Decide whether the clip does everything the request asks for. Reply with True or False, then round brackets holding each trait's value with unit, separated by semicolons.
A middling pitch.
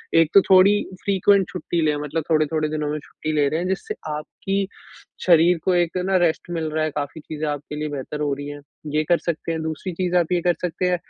True (160 Hz)